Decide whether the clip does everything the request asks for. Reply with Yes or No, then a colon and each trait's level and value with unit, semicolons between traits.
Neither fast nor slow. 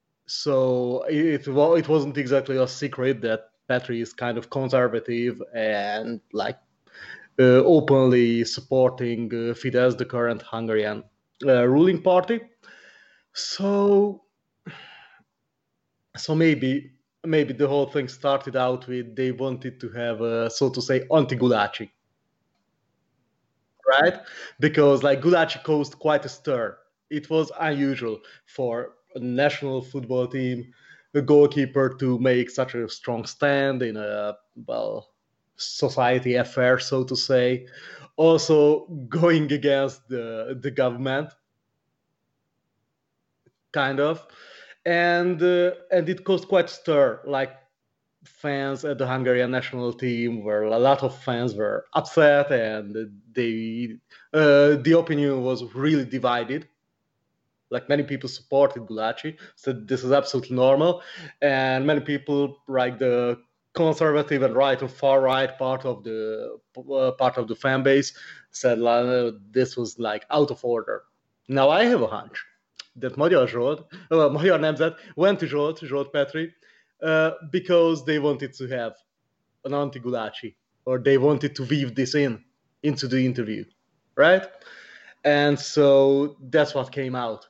No: slow, 130 wpm